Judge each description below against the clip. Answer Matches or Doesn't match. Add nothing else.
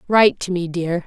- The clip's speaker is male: Doesn't match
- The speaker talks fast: Matches